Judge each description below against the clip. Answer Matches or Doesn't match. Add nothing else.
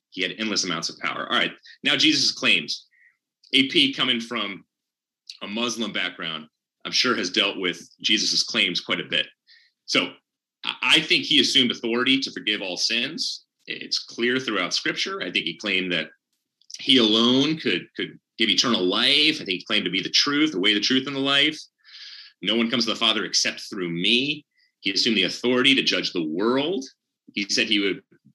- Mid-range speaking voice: Doesn't match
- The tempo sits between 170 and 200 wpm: Matches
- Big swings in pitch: Matches